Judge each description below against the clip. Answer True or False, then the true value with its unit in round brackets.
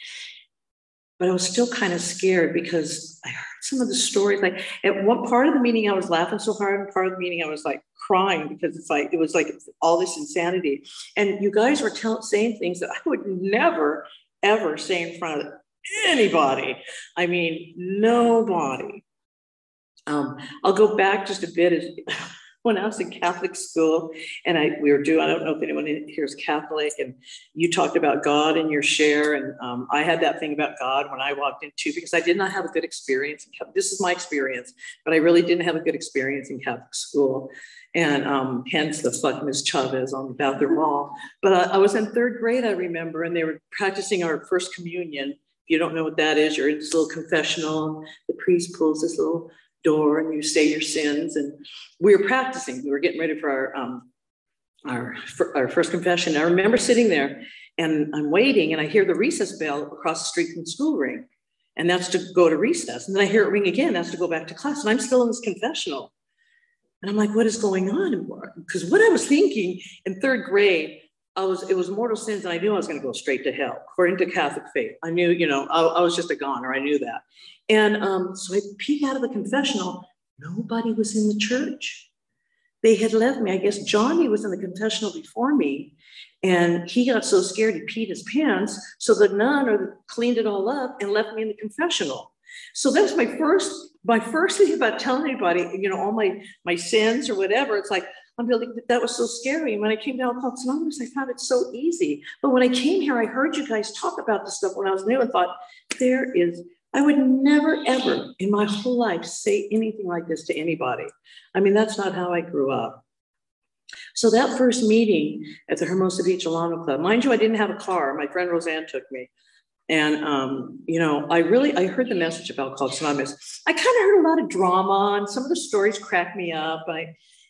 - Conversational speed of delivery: False (225 wpm)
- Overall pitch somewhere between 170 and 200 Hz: True (190 Hz)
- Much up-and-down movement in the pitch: True (6.9 semitones)